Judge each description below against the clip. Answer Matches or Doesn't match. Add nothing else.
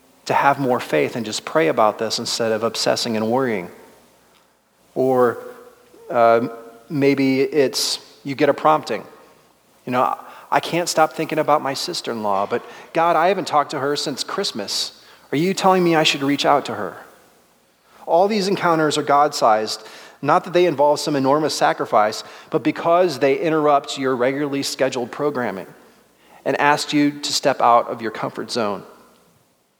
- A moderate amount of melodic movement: Matches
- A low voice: Doesn't match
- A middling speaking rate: Matches